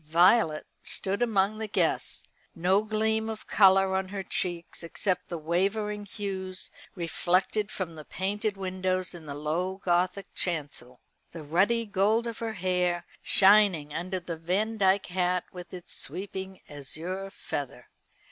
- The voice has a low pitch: No, medium, 185 Hz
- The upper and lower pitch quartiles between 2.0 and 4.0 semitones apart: Yes, average, 2.7 semitones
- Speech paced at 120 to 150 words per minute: Yes, average, 140 wpm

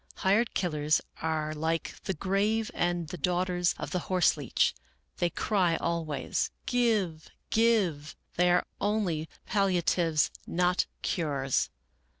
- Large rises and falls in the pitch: No, average, 3.5 semitones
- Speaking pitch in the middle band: Yes, medium, 175 Hz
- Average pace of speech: No, slow, 130 wpm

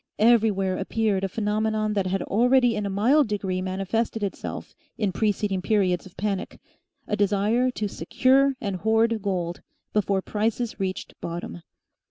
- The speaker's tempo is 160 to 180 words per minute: No, average, 145 wpm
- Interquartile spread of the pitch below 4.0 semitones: Yes, narrow, 2.6 semitones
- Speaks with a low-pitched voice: No, high, 210 Hz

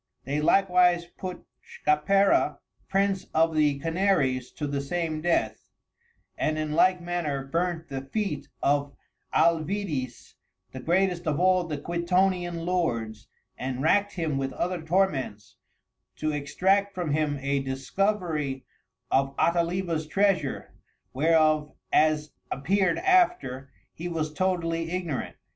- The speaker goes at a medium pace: No, slow, 120 wpm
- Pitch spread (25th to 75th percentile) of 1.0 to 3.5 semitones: No, average, 4.1 semitones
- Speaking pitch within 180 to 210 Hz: No, medium, 165 Hz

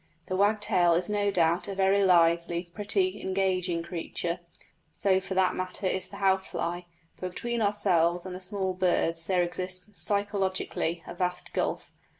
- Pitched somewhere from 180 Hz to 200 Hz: Yes, medium, 185 Hz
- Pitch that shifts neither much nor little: No, narrow, 2.0 semitones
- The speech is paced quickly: No, average, 155 wpm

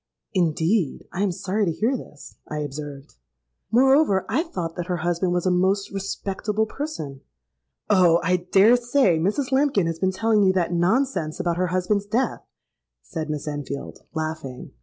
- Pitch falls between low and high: Yes, medium, 180 Hz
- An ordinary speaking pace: Yes, average, 160 wpm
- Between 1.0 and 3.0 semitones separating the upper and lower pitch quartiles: No, average, 4.7 semitones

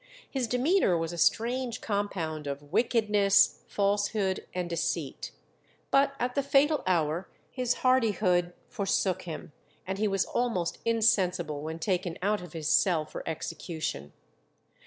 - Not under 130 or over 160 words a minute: Yes, slow, 135 wpm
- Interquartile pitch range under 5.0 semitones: No, average, 5.3 semitones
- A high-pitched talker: Yes, high, 195 Hz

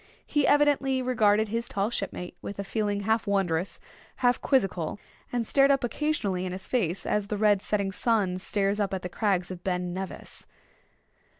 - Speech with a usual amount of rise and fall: Yes, average, 3.8 semitones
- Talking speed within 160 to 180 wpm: Yes, average, 175 wpm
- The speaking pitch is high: Yes, high, 205 Hz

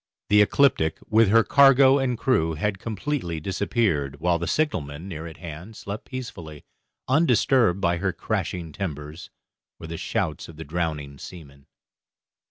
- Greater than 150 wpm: No, average, 145 wpm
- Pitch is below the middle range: Yes, very low, 90 Hz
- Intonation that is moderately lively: No, wide, 6.3 semitones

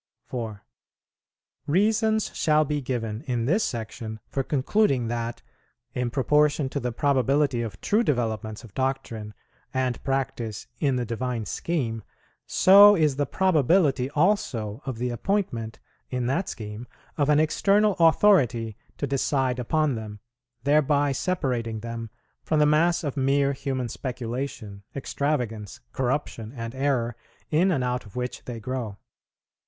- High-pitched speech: No, low, 130 Hz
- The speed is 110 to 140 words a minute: Yes, slow, 135 wpm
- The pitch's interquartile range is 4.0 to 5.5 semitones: Yes, average, 4.3 semitones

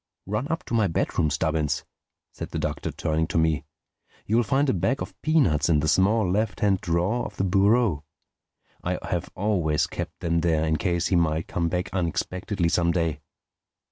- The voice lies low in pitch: Yes, very low, 90 Hz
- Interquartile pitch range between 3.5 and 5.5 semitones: Yes, average, 4.5 semitones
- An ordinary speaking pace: Yes, average, 180 wpm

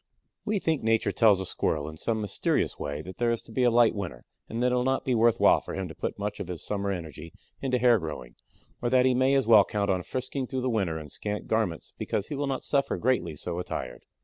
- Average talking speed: No, fast, 255 wpm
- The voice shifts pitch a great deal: Yes, wide, 5.9 semitones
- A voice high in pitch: No, low, 110 Hz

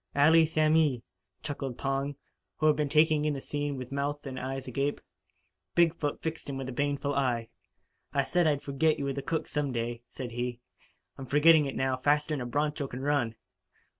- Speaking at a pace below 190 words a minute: No, average, 195 wpm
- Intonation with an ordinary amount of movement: No, narrow, 2.2 semitones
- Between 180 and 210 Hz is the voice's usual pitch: No, medium, 140 Hz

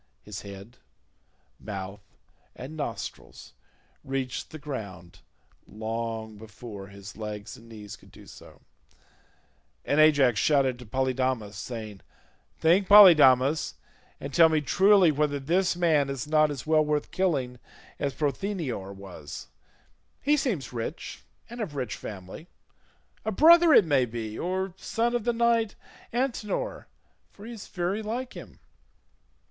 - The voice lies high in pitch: No, medium, 140 Hz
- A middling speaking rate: No, slow, 130 wpm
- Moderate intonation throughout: No, wide, 8.9 semitones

